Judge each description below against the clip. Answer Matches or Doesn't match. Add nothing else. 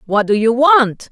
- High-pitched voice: Matches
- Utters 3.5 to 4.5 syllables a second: Matches